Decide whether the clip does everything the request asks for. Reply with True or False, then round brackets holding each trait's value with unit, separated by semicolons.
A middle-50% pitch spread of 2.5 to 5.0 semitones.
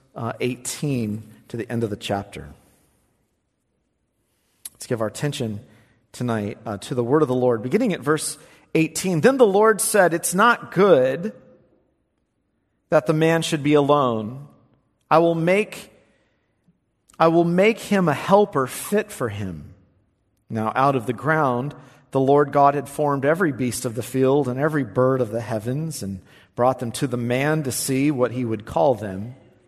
False (5.4 semitones)